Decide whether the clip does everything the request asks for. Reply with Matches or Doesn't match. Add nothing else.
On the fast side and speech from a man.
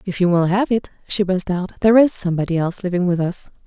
Doesn't match